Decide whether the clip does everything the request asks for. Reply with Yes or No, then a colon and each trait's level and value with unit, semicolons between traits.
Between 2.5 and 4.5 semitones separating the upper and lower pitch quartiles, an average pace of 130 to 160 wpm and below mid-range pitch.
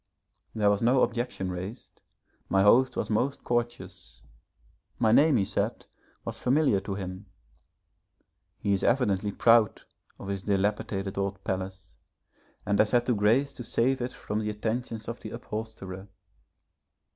Yes: average, 3.6 semitones; average, 145 wpm; low, 105 Hz